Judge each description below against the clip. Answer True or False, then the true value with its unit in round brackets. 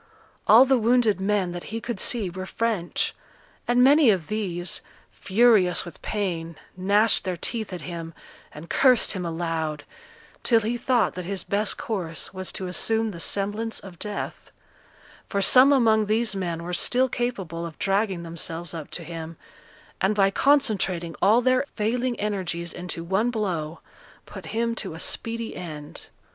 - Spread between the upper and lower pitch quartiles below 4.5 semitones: False (4.8 semitones)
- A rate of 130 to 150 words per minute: False (160 wpm)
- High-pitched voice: True (195 Hz)